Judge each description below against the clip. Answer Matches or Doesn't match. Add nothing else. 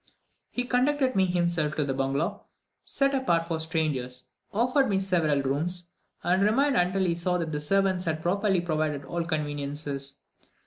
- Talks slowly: Doesn't match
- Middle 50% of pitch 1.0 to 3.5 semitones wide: Doesn't match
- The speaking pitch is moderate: Matches